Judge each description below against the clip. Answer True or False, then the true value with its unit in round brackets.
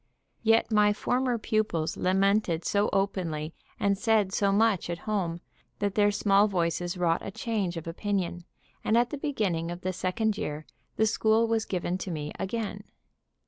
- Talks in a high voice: True (200 Hz)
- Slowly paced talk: False (165 wpm)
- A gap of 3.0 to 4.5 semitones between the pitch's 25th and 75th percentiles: True (3.7 semitones)